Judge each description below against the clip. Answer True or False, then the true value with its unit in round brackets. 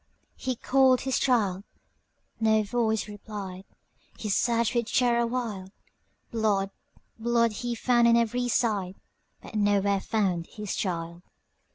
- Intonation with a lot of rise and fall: False (3.1 semitones)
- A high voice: True (220 Hz)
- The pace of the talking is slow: True (100 wpm)